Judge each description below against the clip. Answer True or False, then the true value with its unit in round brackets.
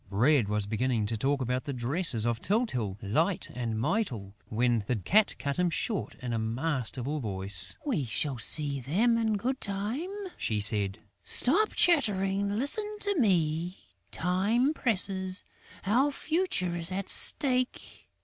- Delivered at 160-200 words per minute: False (145 wpm)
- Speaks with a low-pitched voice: False (165 Hz)